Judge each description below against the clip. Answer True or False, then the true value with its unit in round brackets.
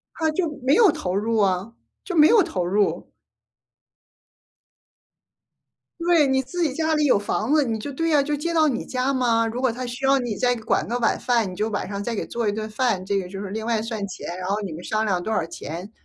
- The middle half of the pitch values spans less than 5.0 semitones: False (5.3 semitones)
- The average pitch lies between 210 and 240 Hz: True (230 Hz)